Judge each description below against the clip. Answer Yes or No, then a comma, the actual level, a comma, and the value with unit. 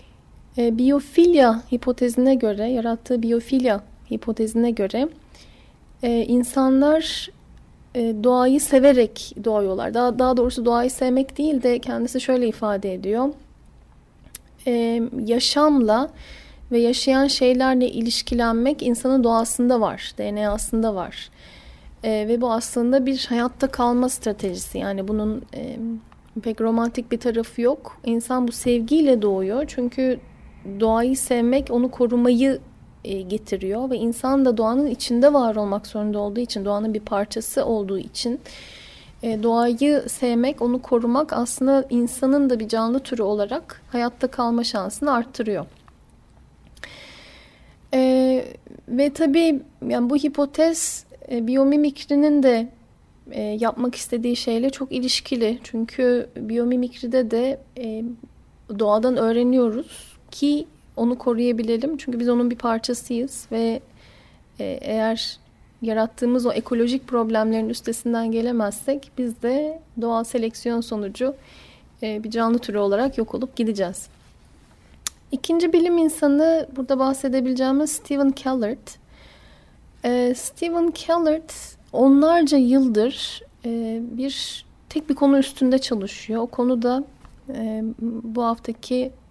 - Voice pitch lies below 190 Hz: No, high, 245 Hz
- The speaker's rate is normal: Yes, average, 110 wpm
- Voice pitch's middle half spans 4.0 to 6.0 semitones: No, narrow, 2.6 semitones